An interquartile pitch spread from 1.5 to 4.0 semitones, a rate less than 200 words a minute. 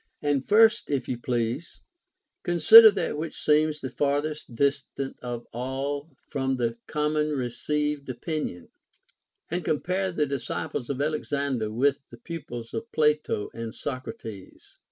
Yes: average, 3.7 semitones; slow, 135 wpm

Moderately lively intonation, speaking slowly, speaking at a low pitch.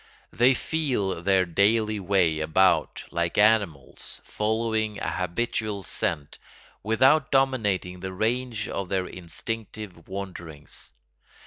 Yes: average, 3.7 semitones; slow, 105 wpm; low, 100 Hz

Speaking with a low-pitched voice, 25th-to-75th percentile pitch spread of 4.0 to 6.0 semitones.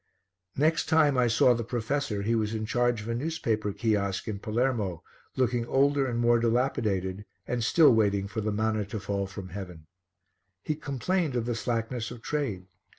No: low, 115 Hz; average, 3.5 semitones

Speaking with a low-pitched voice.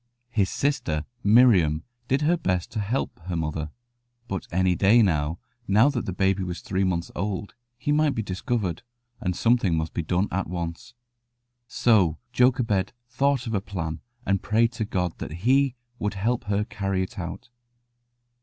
Yes: low, 100 Hz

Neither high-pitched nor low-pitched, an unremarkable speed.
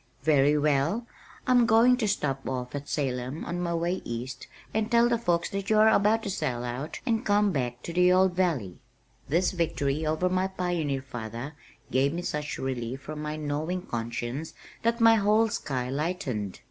Yes: medium, 155 Hz; average, 180 wpm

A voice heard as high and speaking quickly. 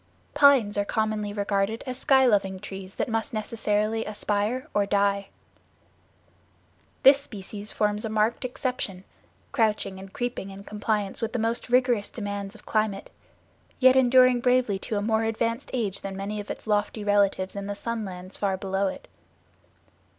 No: high, 210 Hz; average, 160 wpm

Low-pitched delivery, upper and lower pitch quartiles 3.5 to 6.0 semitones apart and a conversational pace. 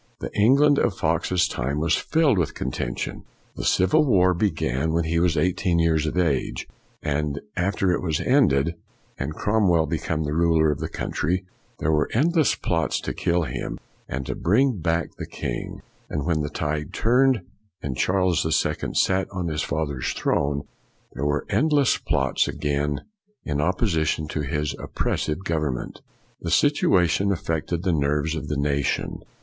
Yes: very low, 80 Hz; average, 3.8 semitones; average, 165 wpm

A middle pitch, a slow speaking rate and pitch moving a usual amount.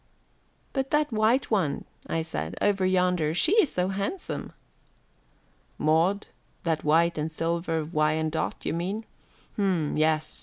Yes: medium, 170 Hz; slow, 125 wpm; average, 4.2 semitones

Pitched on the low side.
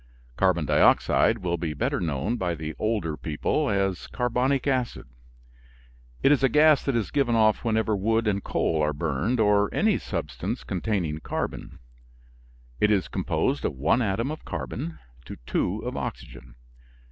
Yes: low, 100 Hz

